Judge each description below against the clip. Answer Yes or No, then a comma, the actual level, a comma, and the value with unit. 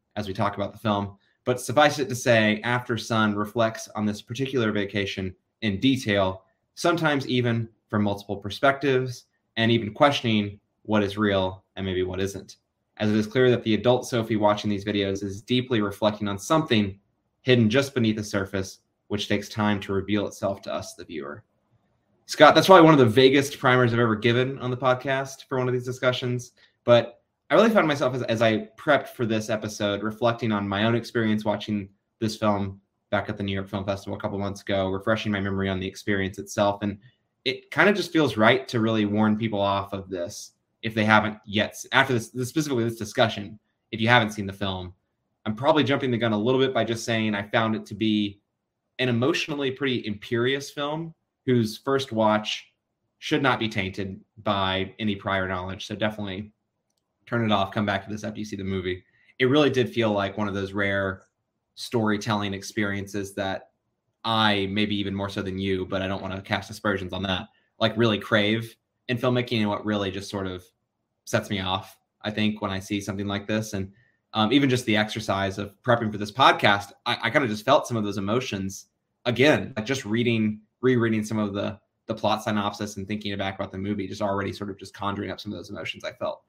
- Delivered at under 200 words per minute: No, fast, 205 wpm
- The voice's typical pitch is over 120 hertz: No, low, 105 Hz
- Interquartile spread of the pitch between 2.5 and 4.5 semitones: Yes, average, 2.8 semitones